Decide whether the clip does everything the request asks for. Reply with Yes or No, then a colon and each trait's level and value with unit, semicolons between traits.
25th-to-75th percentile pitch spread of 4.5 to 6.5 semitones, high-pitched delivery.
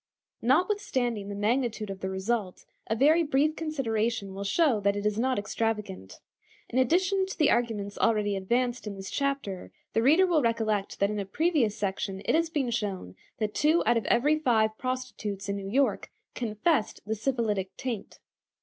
Yes: average, 5.0 semitones; high, 225 Hz